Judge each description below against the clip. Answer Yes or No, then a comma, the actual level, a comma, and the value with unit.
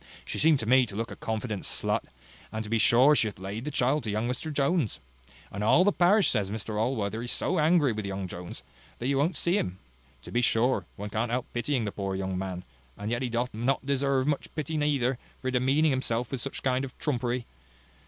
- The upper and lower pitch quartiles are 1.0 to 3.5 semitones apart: No, average, 4.3 semitones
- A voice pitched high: No, low, 125 Hz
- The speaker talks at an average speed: No, fast, 230 wpm